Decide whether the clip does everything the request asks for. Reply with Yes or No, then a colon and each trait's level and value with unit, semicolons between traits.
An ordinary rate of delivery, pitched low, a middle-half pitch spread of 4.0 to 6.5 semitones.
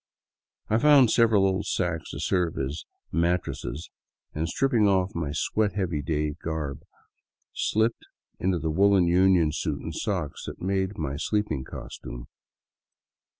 Yes: average, 150 wpm; very low, 90 Hz; average, 4.5 semitones